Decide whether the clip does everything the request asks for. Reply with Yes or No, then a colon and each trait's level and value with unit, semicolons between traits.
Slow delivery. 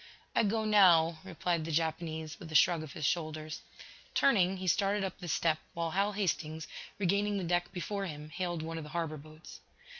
No: average, 190 wpm